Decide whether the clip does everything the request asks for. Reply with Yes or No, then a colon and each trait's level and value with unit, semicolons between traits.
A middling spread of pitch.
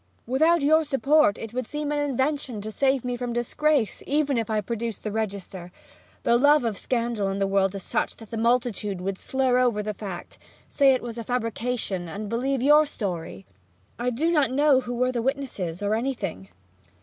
Yes: average, 4.6 semitones